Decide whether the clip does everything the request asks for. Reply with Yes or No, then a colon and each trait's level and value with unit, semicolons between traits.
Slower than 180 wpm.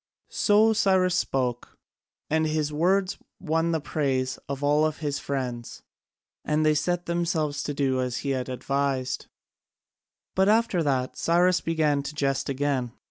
Yes: slow, 135 wpm